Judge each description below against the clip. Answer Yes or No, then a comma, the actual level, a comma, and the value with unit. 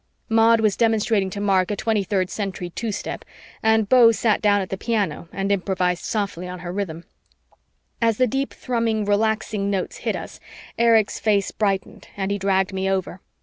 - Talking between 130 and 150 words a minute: No, average, 175 wpm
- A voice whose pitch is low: No, high, 205 Hz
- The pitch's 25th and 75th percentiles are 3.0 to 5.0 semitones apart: No, narrow, 2.6 semitones